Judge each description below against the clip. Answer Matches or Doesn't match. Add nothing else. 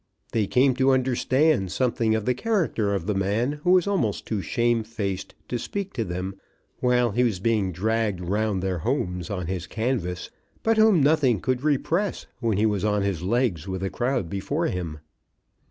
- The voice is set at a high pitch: Doesn't match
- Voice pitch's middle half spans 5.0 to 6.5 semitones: Matches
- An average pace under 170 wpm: Doesn't match